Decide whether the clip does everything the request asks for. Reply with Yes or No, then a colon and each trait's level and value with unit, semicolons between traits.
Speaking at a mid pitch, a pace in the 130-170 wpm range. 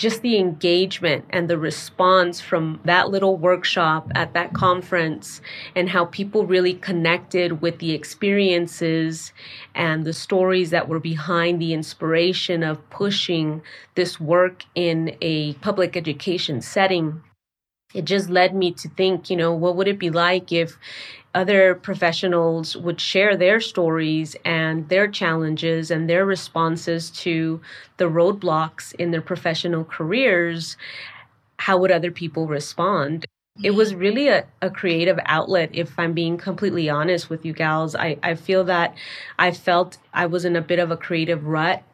Yes: medium, 175 Hz; average, 150 wpm